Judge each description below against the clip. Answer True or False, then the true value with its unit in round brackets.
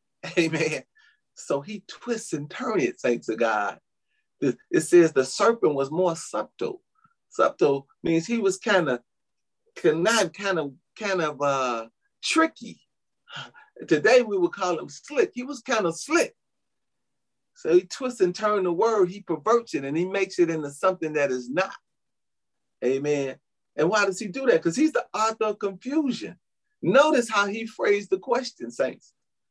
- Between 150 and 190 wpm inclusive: True (165 wpm)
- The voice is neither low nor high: False (205 Hz)